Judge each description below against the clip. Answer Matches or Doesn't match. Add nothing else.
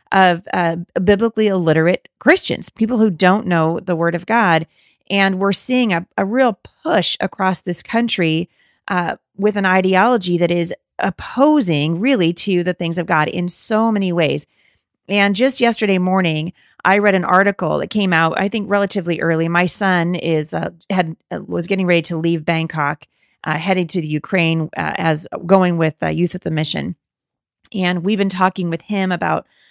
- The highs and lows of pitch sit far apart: Doesn't match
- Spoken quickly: Doesn't match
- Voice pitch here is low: Doesn't match